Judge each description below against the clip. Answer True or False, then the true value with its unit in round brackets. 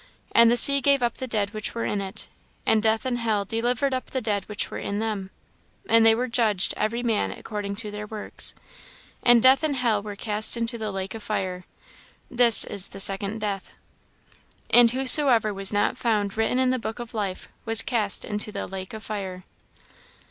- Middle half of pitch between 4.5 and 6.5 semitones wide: False (2.7 semitones)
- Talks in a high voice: True (220 Hz)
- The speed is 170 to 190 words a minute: False (200 wpm)